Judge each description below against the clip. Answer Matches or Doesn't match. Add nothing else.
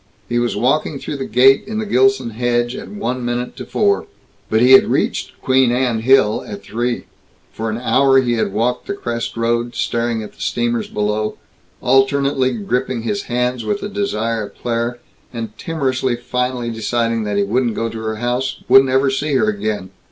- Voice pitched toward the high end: Doesn't match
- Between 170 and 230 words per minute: Matches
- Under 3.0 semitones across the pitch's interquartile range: Matches